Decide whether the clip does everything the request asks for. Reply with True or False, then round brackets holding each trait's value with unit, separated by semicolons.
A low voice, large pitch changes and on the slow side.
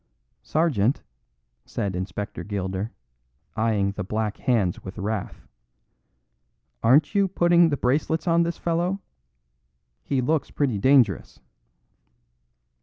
True (120 Hz; 7.9 semitones; 105 wpm)